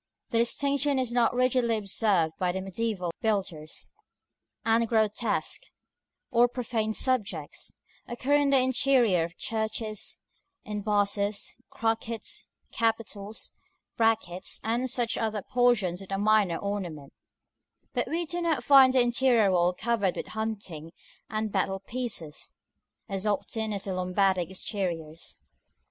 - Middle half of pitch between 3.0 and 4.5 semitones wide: Yes, average, 3.9 semitones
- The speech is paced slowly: Yes, slow, 120 wpm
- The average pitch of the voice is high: Yes, high, 220 Hz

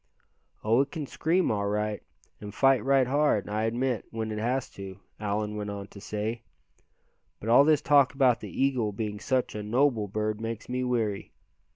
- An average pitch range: Yes, average, 4.0 semitones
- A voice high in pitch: No, low, 115 Hz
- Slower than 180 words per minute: No, average, 185 wpm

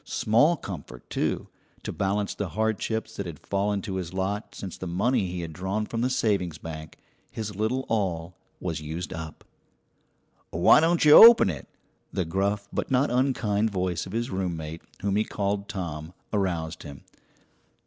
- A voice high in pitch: No, low, 100 Hz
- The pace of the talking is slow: No, average, 165 wpm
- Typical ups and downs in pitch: Yes, average, 4.3 semitones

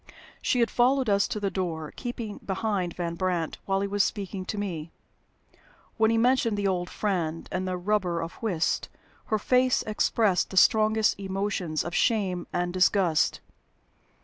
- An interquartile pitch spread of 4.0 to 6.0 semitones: No, average, 3.5 semitones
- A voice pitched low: No, high, 195 Hz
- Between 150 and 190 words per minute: Yes, average, 160 wpm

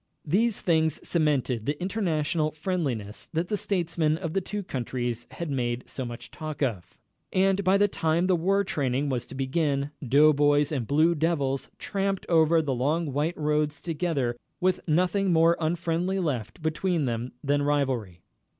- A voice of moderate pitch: Yes, medium, 155 Hz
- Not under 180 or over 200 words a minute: No, average, 160 wpm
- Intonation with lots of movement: No, average, 4.1 semitones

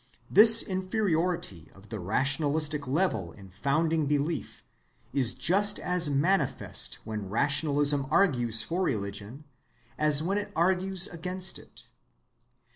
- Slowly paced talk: Yes, slow, 115 wpm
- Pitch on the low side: No, medium, 150 Hz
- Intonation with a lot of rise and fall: Yes, wide, 6.7 semitones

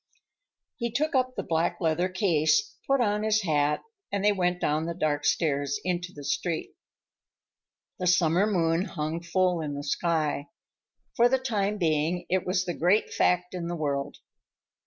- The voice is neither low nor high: Yes, medium, 175 Hz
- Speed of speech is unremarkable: Yes, average, 165 wpm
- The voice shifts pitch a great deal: No, average, 4.1 semitones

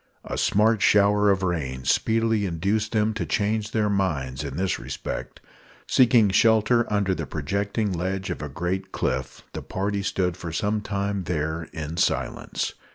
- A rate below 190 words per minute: Yes, average, 160 wpm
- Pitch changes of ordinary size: Yes, average, 3.5 semitones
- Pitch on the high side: No, low, 100 Hz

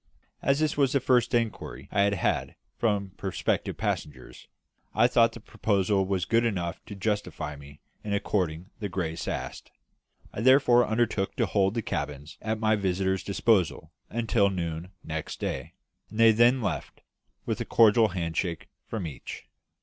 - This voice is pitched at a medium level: No, low, 100 Hz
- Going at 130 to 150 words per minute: No, average, 160 wpm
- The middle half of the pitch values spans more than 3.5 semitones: Yes, average, 4.3 semitones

